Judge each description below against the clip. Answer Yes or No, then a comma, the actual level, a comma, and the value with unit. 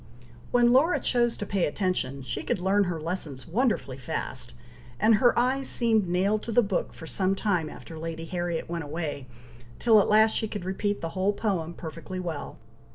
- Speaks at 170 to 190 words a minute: Yes, average, 185 wpm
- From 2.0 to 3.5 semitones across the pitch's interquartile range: No, average, 4.7 semitones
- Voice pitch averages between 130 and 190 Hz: Yes, medium, 185 Hz